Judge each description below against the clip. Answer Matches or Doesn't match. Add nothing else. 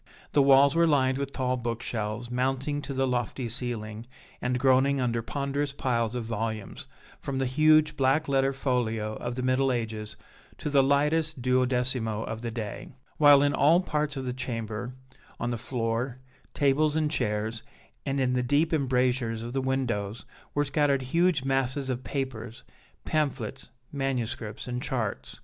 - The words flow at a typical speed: Matches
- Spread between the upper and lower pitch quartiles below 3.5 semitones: Matches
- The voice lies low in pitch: Matches